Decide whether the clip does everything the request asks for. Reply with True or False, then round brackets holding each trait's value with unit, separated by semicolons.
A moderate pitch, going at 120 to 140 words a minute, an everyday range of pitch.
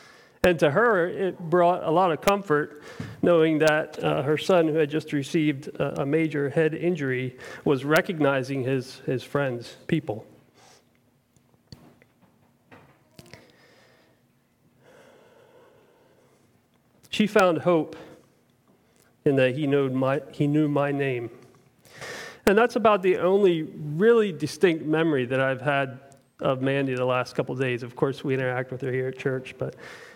True (150 Hz; 135 wpm; 4.7 semitones)